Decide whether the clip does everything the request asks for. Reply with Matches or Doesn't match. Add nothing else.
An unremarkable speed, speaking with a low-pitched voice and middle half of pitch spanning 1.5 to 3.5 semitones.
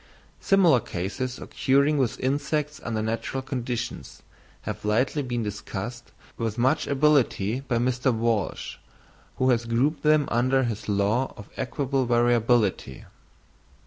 Doesn't match